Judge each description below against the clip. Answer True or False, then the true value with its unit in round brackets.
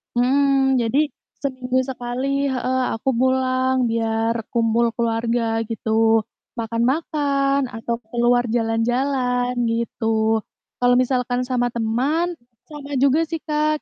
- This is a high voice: True (250 Hz)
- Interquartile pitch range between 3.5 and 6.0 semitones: False (2.9 semitones)